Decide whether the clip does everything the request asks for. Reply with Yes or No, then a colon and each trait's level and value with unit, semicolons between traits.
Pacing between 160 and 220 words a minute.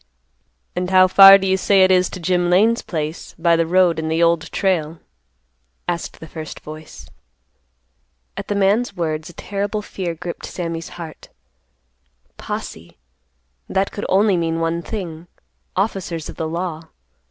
No: average, 150 wpm